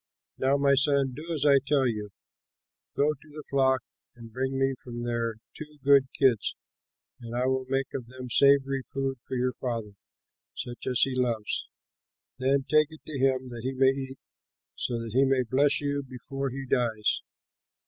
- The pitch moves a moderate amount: No, narrow, 2.0 semitones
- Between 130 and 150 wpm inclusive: No, average, 180 wpm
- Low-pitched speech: Yes, low, 130 Hz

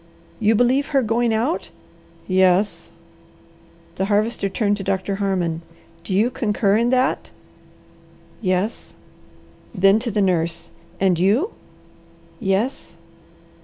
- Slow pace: Yes, slow, 110 wpm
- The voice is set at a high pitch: Yes, high, 205 Hz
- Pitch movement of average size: Yes, average, 3.7 semitones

